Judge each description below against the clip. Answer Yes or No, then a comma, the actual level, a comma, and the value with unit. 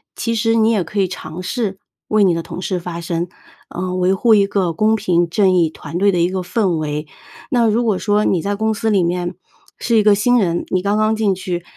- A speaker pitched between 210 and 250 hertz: No, high, 190 Hz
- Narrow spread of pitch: No, average, 3.6 semitones